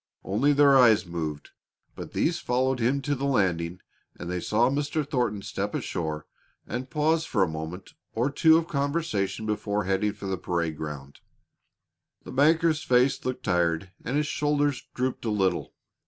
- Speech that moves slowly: No, average, 165 wpm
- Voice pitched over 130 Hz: No, low, 115 Hz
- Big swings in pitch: Yes, wide, 7.5 semitones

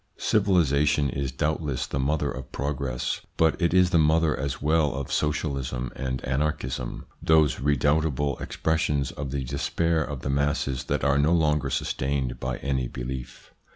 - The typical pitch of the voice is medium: No, very low, 70 Hz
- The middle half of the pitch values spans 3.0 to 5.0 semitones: No, narrow, 2.6 semitones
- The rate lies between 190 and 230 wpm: No, average, 155 wpm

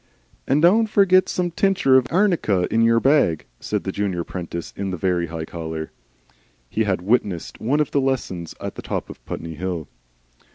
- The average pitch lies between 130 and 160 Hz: No, low, 105 Hz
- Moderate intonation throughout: No, wide, 9.0 semitones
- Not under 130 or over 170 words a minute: No, average, 180 wpm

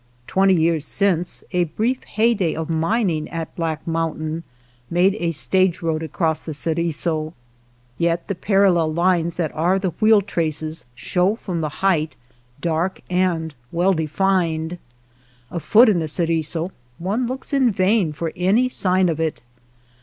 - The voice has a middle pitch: Yes, medium, 170 Hz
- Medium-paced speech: Yes, average, 150 wpm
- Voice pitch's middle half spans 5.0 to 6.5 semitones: No, average, 3.1 semitones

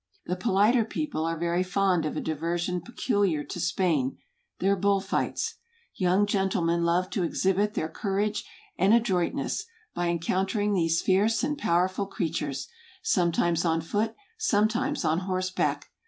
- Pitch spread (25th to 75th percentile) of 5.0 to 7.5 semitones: No, average, 3.3 semitones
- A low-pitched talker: No, medium, 185 Hz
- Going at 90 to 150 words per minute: Yes, average, 145 wpm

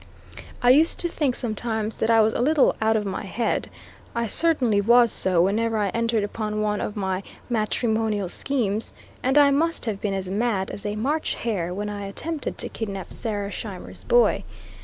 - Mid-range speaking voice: No, high, 220 Hz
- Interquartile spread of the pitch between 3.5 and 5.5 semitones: No, average, 3.1 semitones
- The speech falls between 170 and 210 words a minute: Yes, average, 185 wpm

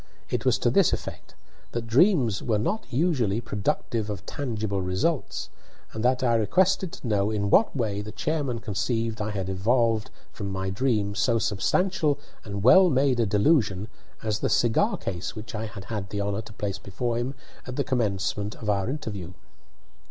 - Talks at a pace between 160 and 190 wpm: Yes, average, 175 wpm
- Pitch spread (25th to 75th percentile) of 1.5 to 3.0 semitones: No, average, 4.0 semitones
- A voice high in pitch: No, low, 110 Hz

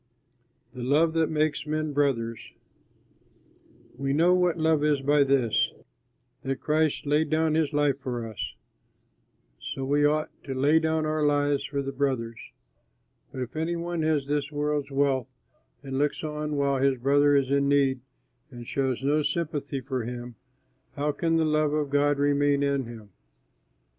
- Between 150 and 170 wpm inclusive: Yes, average, 160 wpm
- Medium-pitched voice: Yes, medium, 145 Hz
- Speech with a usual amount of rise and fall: No, narrow, 2.1 semitones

